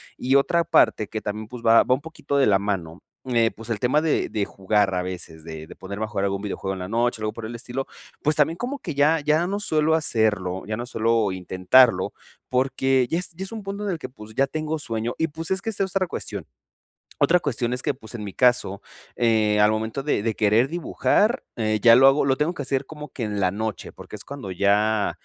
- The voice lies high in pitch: No, low, 120 Hz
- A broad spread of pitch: Yes, wide, 6.1 semitones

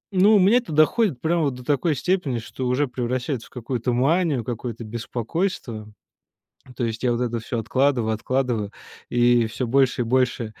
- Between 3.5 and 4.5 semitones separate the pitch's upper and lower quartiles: Yes, average, 3.8 semitones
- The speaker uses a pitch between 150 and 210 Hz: No, low, 125 Hz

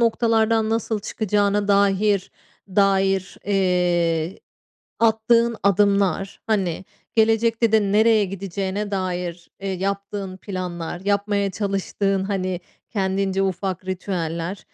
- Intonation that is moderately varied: No, narrow, 2.0 semitones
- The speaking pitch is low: No, high, 195 Hz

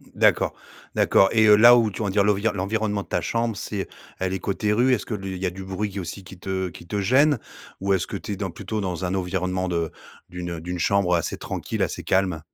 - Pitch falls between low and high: No, very low, 95 Hz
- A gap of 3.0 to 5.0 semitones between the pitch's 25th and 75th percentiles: No, narrow, 2.4 semitones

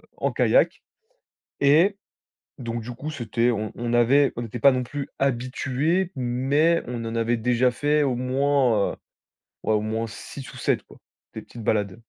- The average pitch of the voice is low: Yes, low, 125 Hz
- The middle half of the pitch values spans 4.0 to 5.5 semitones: No, average, 3.3 semitones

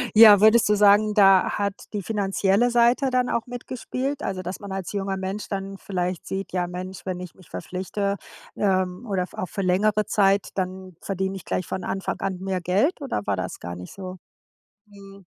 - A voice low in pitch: No, high, 195 Hz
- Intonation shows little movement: Yes, narrow, 2.1 semitones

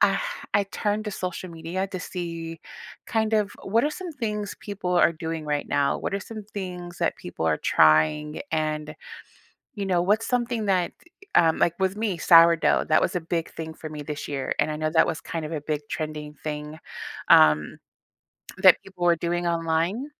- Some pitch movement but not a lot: Yes, average, 4.3 semitones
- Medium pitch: Yes, medium, 170 Hz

